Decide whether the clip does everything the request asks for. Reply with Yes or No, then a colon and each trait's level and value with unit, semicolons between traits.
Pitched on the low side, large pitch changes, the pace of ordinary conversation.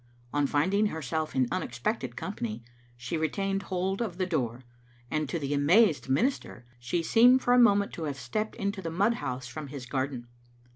No: medium, 160 Hz; wide, 7.1 semitones; average, 180 wpm